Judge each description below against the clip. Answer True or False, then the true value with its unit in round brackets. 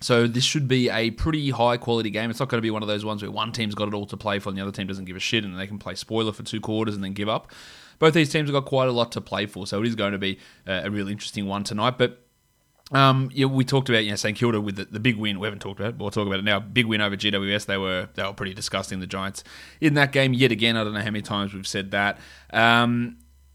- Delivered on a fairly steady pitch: False (3.2 semitones)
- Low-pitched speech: True (105 Hz)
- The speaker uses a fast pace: True (310 wpm)